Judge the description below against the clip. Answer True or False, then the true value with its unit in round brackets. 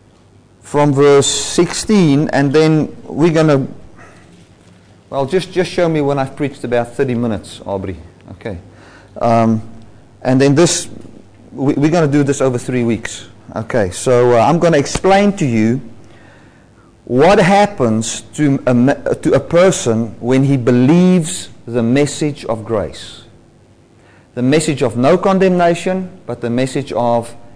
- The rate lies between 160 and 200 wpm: False (145 wpm)